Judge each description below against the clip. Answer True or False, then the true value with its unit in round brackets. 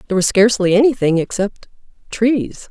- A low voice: False (210 Hz)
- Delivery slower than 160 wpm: True (135 wpm)